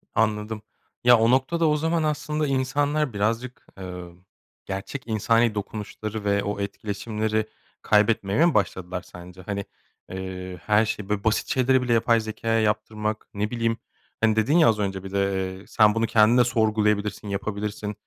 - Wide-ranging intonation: No, narrow, 2.6 semitones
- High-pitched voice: No, low, 110 Hz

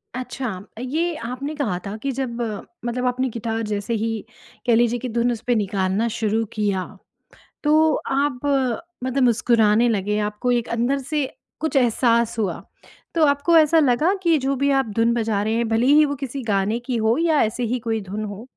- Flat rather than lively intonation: No, average, 3.7 semitones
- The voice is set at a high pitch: Yes, high, 240 Hz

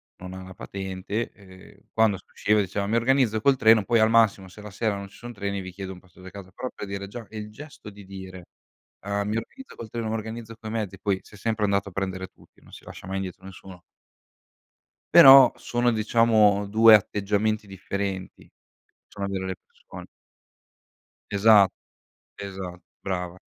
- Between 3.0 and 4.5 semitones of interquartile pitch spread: No, narrow, 2.6 semitones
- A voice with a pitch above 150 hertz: No, low, 100 Hz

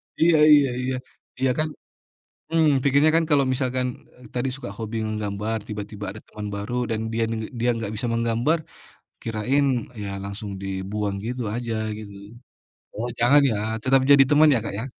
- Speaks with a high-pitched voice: No, low, 115 Hz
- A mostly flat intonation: No, average, 4.1 semitones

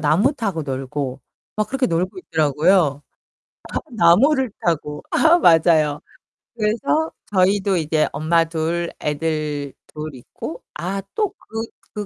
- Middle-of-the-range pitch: Yes, medium, 165 Hz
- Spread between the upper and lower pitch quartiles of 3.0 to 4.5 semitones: No, wide, 5.6 semitones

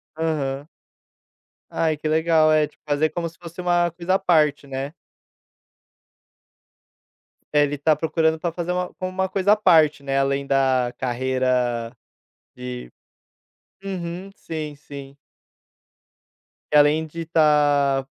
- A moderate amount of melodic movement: Yes, average, 3.5 semitones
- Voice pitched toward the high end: No, medium, 155 Hz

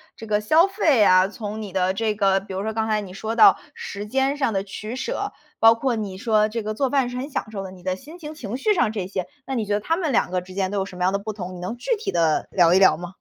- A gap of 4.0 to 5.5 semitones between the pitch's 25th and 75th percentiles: Yes, average, 4.7 semitones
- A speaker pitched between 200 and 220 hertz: Yes, high, 215 Hz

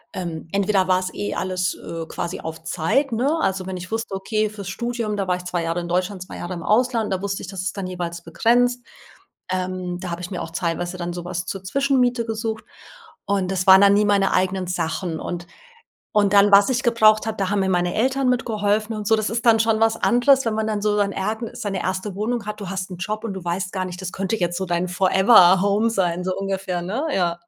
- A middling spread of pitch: Yes, average, 3.2 semitones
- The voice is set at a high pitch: Yes, high, 195 Hz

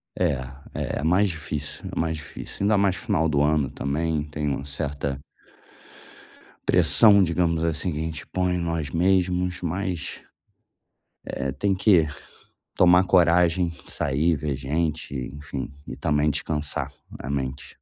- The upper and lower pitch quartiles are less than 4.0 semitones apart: Yes, average, 3.5 semitones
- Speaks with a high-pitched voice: No, very low, 80 Hz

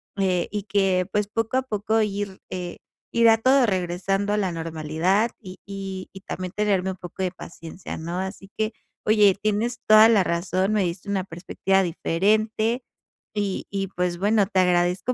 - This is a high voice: Yes, high, 195 Hz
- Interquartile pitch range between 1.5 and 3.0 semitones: Yes, average, 2.7 semitones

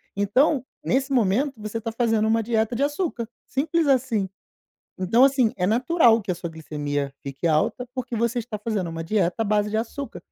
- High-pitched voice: Yes, high, 225 Hz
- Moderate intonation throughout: Yes, average, 4.8 semitones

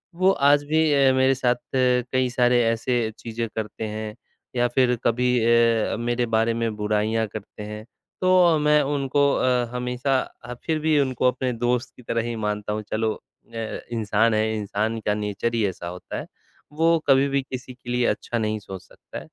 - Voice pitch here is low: Yes, low, 120 Hz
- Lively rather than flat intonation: No, average, 3.1 semitones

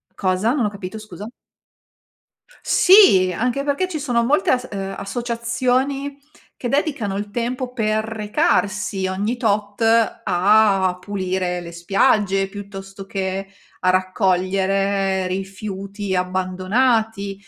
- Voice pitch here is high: Yes, high, 200 Hz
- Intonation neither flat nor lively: Yes, average, 3.7 semitones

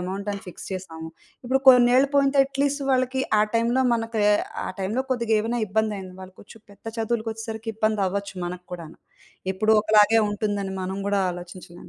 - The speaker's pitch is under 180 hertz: No, high, 215 Hz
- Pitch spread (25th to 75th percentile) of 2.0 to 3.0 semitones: No, average, 3.7 semitones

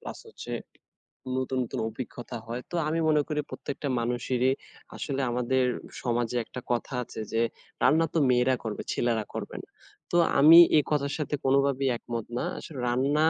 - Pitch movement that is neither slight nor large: Yes, average, 3.2 semitones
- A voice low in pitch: Yes, low, 130 Hz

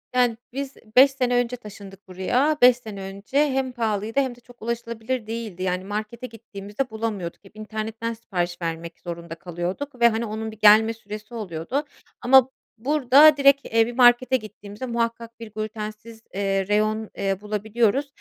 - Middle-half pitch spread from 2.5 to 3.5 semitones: Yes, average, 3.2 semitones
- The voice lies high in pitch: Yes, high, 220 Hz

